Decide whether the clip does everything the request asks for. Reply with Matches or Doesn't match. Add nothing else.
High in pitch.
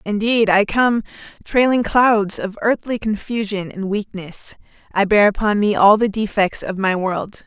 Matches